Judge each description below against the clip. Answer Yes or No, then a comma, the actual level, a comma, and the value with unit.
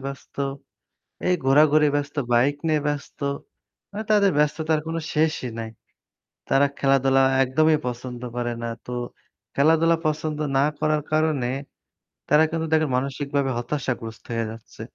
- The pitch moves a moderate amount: Yes, average, 3.1 semitones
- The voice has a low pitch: No, medium, 145 Hz